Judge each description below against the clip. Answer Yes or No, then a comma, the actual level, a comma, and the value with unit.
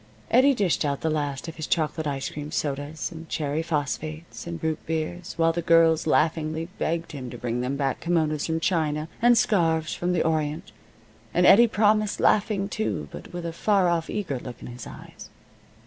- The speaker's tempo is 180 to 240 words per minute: Yes, average, 190 wpm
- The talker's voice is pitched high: No, medium, 160 Hz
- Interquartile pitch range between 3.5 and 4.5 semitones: No, average, 2.7 semitones